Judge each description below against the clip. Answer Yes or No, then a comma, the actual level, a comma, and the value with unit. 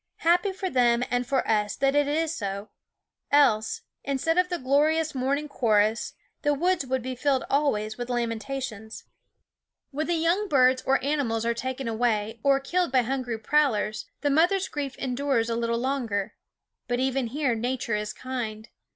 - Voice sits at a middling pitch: No, very high, 260 Hz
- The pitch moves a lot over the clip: No, average, 4.0 semitones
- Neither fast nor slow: Yes, average, 165 wpm